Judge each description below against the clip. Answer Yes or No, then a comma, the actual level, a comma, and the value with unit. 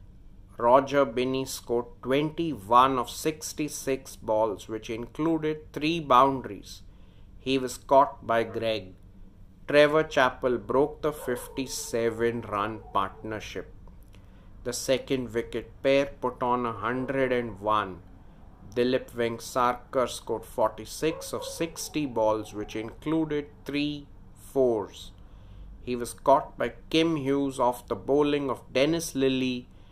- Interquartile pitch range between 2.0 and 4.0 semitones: No, average, 5.0 semitones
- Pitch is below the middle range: Yes, low, 120 Hz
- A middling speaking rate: No, slow, 105 wpm